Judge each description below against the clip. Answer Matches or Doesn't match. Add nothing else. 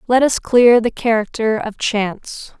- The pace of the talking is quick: Doesn't match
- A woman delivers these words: Matches